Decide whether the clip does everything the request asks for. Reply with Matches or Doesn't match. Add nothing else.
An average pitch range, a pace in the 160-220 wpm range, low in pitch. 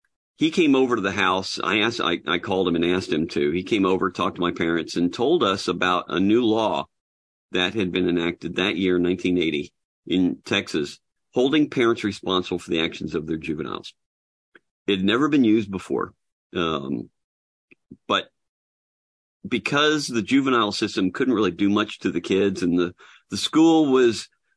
Matches